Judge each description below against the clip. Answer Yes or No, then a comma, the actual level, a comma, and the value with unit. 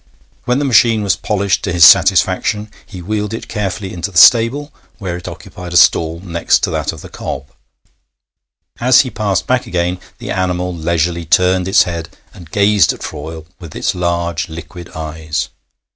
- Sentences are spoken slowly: No, average, 175 wpm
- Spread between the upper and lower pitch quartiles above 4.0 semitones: No, average, 3.6 semitones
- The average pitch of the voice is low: Yes, very low, 90 Hz